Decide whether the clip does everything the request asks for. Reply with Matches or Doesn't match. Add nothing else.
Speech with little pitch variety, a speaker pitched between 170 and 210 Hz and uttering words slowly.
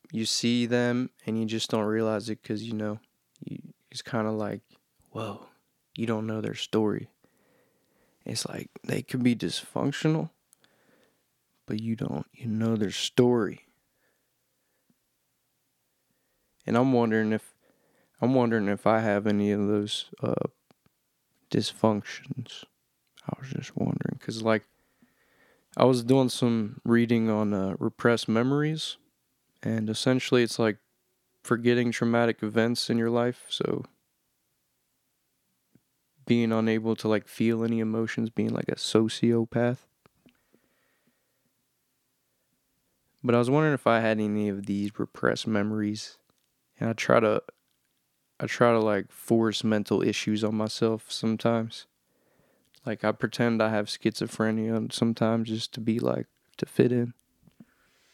Doesn't match